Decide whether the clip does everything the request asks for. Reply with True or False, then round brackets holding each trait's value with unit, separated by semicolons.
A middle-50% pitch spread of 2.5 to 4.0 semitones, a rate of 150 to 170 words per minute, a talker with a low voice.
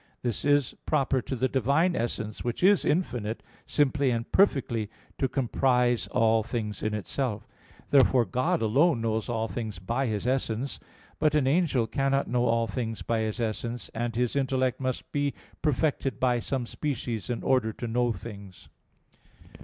True (3.3 semitones; 160 wpm; 125 Hz)